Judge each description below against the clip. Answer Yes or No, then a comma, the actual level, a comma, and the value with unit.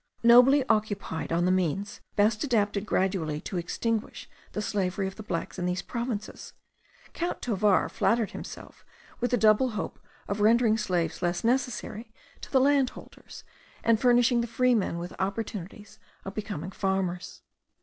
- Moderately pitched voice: No, high, 210 Hz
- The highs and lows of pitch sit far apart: No, average, 3.7 semitones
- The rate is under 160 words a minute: Yes, average, 145 wpm